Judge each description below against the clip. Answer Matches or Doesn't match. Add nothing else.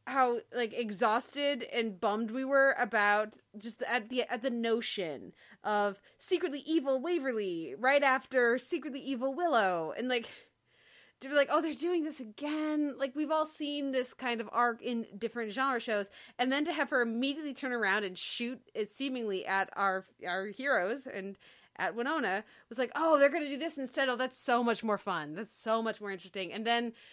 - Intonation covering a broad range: Doesn't match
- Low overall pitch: Doesn't match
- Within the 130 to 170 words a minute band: Doesn't match